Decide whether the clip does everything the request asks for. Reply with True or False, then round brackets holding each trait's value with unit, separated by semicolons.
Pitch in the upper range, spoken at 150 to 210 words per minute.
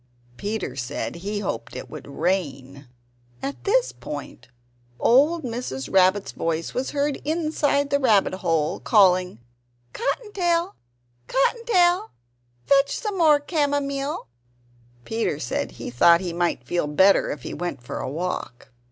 False (210 Hz; 140 wpm)